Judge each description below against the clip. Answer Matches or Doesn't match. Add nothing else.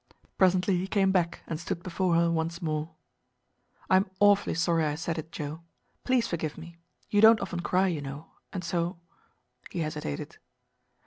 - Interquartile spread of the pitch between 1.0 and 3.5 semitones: Matches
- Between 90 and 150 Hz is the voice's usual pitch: Doesn't match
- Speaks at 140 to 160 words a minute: Doesn't match